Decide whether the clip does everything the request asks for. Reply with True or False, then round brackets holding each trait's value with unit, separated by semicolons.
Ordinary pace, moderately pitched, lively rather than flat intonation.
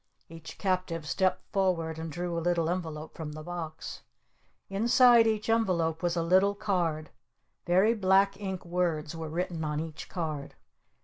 False (150 wpm; 175 Hz; 3.0 semitones)